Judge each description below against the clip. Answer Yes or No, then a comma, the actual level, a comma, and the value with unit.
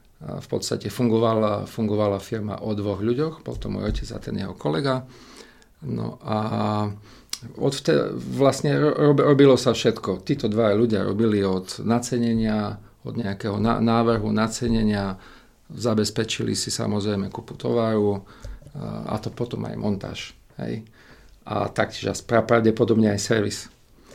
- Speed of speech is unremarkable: Yes, average, 135 wpm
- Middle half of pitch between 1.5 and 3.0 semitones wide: Yes, narrow, 2.4 semitones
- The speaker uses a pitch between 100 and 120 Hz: Yes, low, 115 Hz